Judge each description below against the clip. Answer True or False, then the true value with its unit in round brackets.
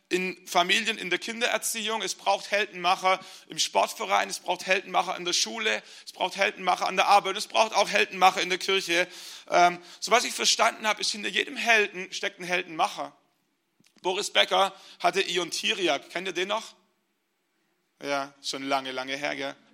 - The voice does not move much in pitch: True (2.3 semitones)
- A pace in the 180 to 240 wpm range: False (170 wpm)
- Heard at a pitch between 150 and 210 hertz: True (185 Hz)